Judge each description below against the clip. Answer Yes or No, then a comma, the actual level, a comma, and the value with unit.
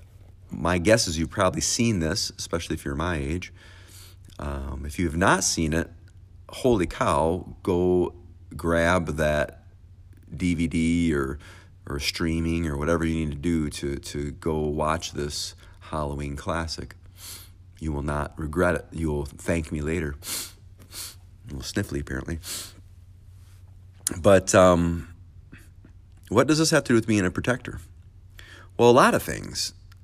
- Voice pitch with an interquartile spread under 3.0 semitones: Yes, narrow, 2.4 semitones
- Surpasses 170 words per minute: No, average, 145 wpm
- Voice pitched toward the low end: Yes, very low, 90 Hz